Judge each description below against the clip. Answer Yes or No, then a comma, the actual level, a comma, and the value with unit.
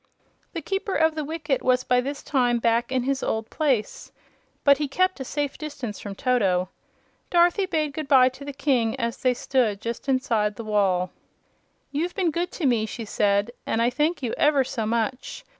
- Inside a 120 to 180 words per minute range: No, average, 190 wpm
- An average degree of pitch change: Yes, average, 4.5 semitones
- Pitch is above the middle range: Yes, very high, 260 Hz